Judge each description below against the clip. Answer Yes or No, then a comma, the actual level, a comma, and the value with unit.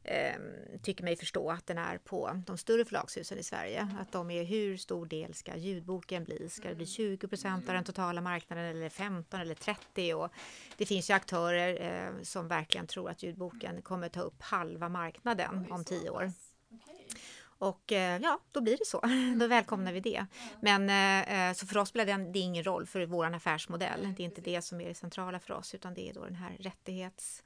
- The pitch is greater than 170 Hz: Yes, medium, 185 Hz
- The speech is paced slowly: No, fast, 195 wpm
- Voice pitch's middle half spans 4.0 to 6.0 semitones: No, narrow, 2.4 semitones